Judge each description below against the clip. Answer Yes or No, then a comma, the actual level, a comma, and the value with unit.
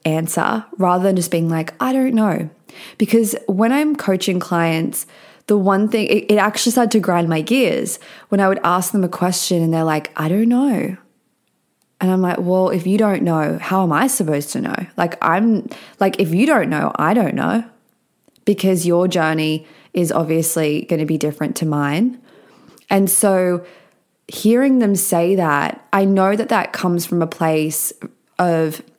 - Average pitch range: Yes, average, 4.7 semitones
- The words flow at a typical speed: Yes, average, 180 wpm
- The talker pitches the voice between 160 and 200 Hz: Yes, medium, 185 Hz